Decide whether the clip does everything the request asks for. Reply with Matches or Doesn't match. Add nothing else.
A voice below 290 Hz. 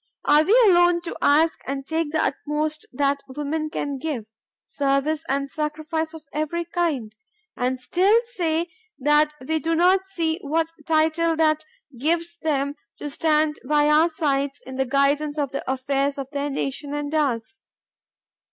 Doesn't match